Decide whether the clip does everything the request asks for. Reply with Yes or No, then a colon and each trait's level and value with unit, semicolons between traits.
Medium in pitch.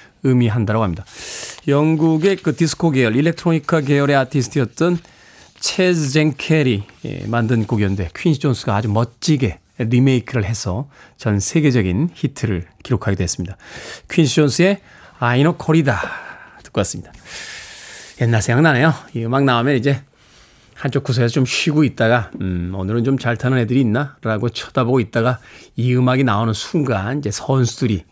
No: low, 130 Hz